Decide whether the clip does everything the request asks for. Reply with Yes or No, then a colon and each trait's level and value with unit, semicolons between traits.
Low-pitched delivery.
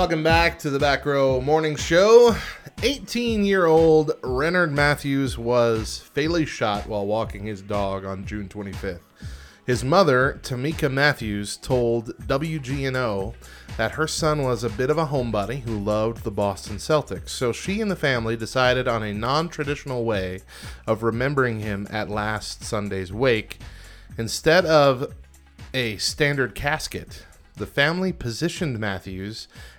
Yes: low, 120 Hz